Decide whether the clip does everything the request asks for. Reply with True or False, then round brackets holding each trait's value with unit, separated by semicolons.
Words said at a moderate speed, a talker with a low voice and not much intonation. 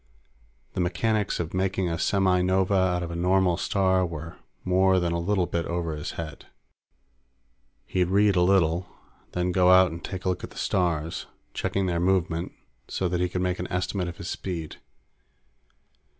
True (180 wpm; 90 Hz; 1.7 semitones)